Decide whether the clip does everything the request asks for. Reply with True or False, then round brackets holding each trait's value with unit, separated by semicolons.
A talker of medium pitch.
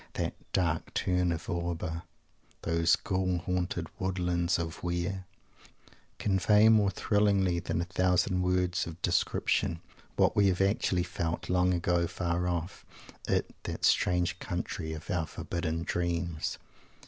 False (90 Hz)